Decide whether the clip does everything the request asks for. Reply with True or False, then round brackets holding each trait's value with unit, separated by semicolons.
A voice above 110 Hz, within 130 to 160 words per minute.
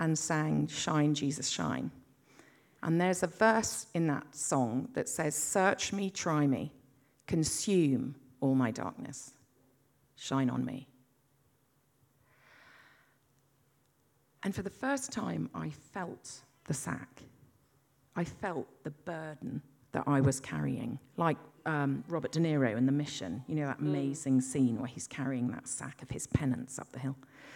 True (140 Hz; 145 wpm)